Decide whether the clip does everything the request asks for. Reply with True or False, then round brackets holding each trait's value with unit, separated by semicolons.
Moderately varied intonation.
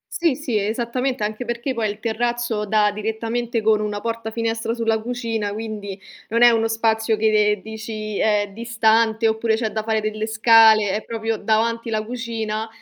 False (1.2 semitones)